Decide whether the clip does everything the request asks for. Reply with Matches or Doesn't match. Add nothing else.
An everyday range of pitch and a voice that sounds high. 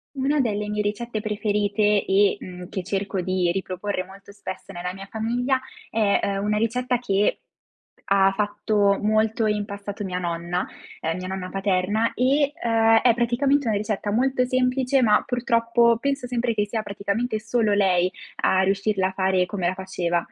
Matches